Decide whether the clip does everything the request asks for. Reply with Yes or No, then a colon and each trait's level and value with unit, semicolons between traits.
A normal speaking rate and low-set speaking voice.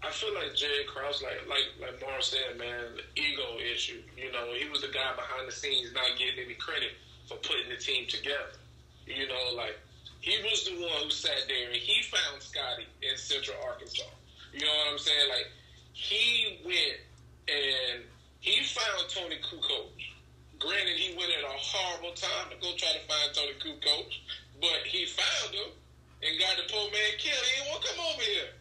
No: average, 190 wpm; medium, 145 Hz